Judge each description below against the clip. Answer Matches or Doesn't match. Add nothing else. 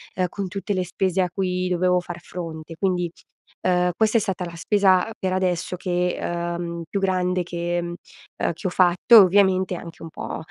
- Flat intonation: Matches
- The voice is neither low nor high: Matches